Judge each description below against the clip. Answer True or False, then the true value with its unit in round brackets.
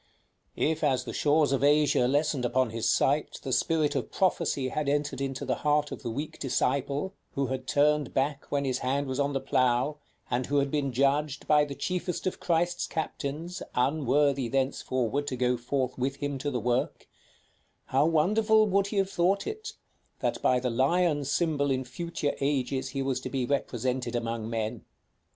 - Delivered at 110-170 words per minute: False (180 wpm)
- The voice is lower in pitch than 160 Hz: True (140 Hz)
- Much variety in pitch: False (2.7 semitones)